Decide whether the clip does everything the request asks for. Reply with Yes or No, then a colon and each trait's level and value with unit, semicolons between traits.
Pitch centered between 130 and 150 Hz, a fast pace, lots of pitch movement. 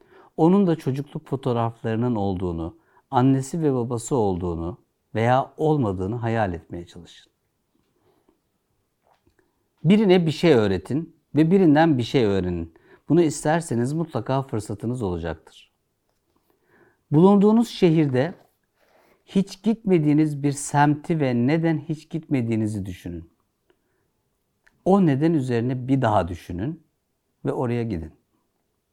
No: low, 135 Hz; average, 100 wpm; wide, 6.7 semitones